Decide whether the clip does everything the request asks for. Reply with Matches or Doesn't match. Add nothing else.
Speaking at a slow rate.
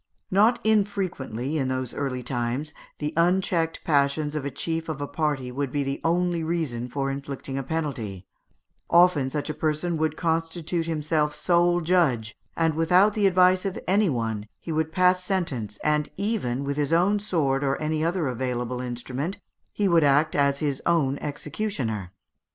Doesn't match